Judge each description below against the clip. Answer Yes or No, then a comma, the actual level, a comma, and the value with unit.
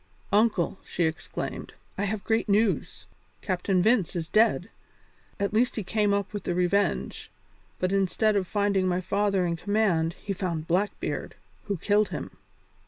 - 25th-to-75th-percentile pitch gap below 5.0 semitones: Yes, narrow, 2.6 semitones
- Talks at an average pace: Yes, average, 155 wpm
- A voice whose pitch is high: Yes, high, 200 Hz